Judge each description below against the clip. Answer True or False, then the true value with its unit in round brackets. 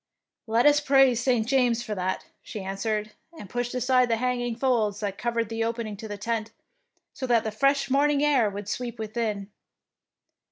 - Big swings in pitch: False (2.8 semitones)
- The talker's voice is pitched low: False (230 Hz)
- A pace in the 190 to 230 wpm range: False (175 wpm)